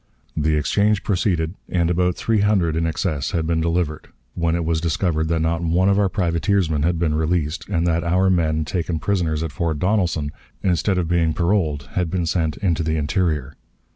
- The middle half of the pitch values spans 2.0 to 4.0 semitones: Yes, narrow, 2.4 semitones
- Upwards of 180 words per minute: Yes, average, 190 wpm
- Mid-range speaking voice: No, very low, 85 Hz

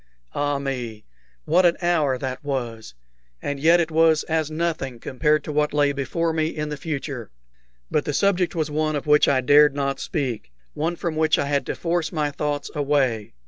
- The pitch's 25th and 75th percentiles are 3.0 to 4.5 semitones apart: No, narrow, 2.5 semitones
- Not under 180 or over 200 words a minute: Yes, average, 190 wpm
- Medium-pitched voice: Yes, medium, 150 Hz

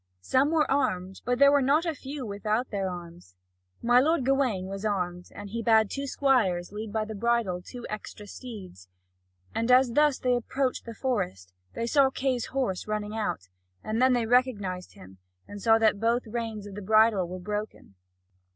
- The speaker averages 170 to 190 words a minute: Yes, average, 180 wpm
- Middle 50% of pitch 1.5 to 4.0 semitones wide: No, average, 4.5 semitones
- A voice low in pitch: No, high, 220 Hz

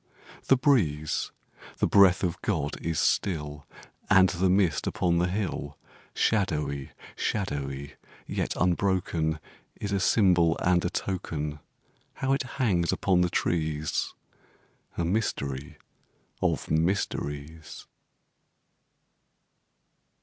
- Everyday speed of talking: No, slow, 100 wpm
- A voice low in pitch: Yes, very low, 85 Hz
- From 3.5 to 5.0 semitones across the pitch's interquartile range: Yes, average, 4.1 semitones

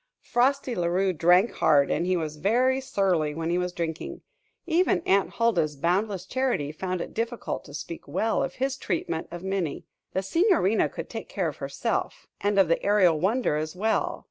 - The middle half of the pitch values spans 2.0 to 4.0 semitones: No, average, 5.3 semitones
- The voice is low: No, medium, 185 Hz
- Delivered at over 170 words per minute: Yes, average, 185 wpm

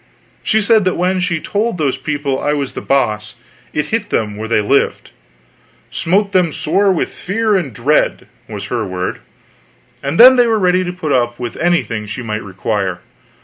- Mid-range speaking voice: Yes, medium, 150 Hz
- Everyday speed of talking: Yes, average, 185 wpm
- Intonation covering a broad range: Yes, wide, 8.3 semitones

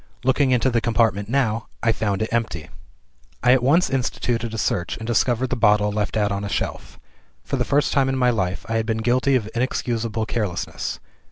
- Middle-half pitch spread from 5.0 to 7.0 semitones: No, average, 3.0 semitones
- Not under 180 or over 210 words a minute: Yes, average, 200 wpm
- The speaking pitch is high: No, low, 115 Hz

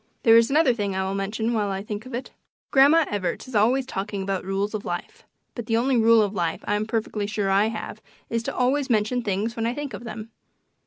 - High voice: Yes, high, 220 Hz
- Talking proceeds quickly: Yes, fast, 230 wpm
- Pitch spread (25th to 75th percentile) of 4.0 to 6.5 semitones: No, average, 2.9 semitones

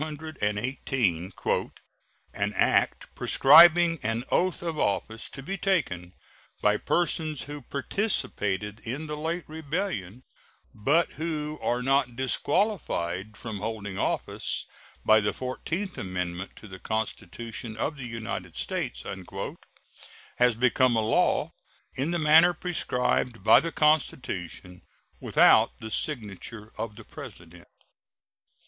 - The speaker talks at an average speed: No, slow, 115 wpm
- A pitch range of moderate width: No, wide, 7.0 semitones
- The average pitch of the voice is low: Yes, low, 125 Hz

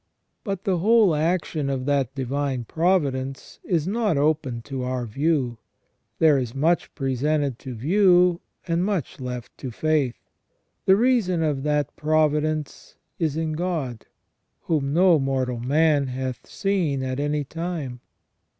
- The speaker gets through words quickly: No, slow, 135 wpm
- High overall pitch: No, medium, 150 Hz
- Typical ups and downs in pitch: Yes, average, 4.2 semitones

